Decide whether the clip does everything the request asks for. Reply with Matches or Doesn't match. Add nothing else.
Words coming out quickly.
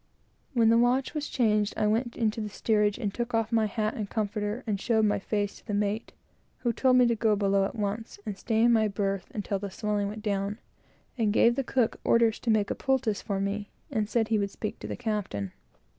Matches